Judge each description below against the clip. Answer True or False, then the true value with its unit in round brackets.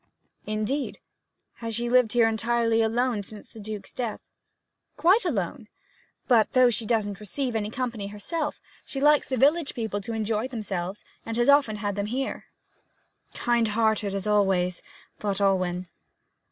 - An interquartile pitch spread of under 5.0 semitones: True (3.2 semitones)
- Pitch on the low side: False (225 Hz)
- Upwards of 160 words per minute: False (140 wpm)